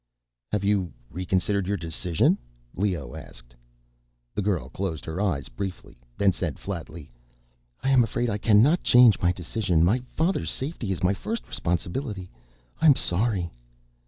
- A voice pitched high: No, very low, 95 Hz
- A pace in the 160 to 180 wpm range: No, average, 145 wpm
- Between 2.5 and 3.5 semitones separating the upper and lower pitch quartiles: No, average, 4.0 semitones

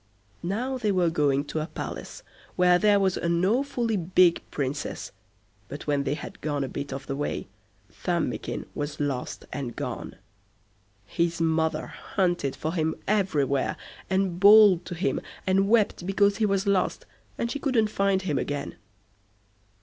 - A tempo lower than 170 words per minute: Yes, average, 155 wpm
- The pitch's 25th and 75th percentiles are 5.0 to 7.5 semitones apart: Yes, average, 5.3 semitones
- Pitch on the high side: No, medium, 175 Hz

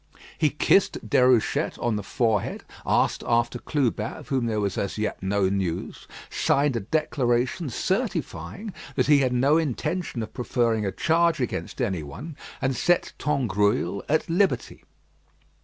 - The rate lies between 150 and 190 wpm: No, average, 140 wpm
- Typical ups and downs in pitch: No, wide, 6.1 semitones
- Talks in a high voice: No, low, 125 Hz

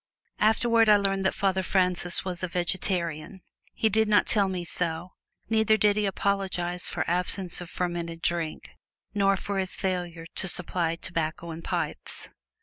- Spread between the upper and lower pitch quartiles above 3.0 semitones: No, narrow, 2.4 semitones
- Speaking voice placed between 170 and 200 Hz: Yes, medium, 185 Hz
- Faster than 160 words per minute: No, average, 155 wpm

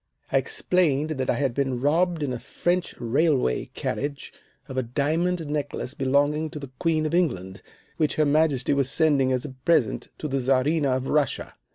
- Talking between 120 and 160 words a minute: No, average, 180 wpm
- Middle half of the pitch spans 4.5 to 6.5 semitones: No, average, 3.3 semitones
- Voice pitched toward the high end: No, medium, 145 Hz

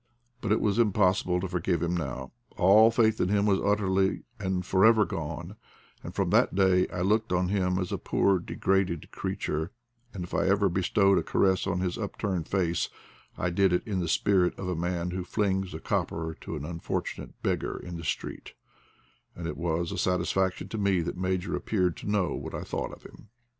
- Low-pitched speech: Yes, very low, 95 Hz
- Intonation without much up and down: Yes, narrow, 2.1 semitones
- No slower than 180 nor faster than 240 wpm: Yes, average, 200 wpm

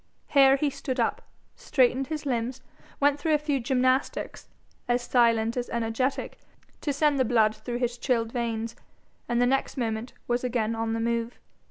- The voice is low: No, high, 245 Hz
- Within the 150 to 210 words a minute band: Yes, average, 170 wpm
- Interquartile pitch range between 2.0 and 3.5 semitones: Yes, average, 2.7 semitones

